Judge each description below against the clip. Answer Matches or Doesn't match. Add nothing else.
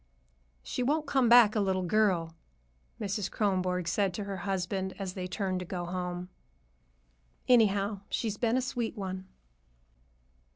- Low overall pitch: Doesn't match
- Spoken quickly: Doesn't match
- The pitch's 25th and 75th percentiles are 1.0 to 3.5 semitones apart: Matches